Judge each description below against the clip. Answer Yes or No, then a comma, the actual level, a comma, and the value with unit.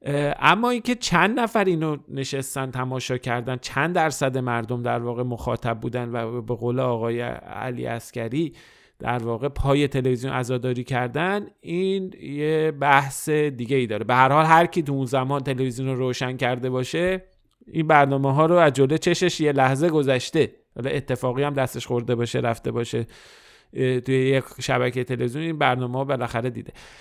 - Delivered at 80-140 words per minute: No, fast, 155 wpm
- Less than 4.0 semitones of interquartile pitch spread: Yes, average, 3.4 semitones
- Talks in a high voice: No, low, 130 Hz